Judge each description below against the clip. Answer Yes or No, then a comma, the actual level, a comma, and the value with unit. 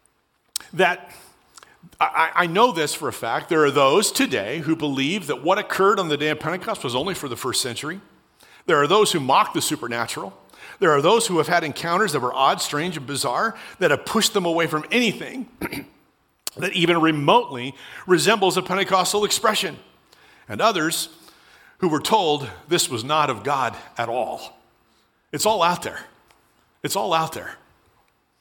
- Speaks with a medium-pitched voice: Yes, medium, 170 Hz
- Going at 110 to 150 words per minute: No, average, 175 wpm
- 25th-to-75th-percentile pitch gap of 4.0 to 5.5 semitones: Yes, average, 4.7 semitones